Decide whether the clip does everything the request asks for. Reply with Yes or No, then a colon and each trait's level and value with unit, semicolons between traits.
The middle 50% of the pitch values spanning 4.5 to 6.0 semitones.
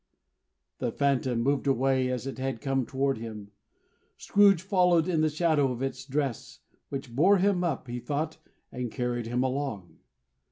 No: average, 3.7 semitones